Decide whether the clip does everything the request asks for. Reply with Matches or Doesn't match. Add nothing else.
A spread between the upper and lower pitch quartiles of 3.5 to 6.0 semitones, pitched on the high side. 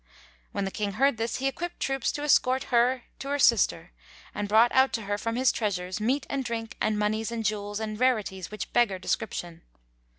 Matches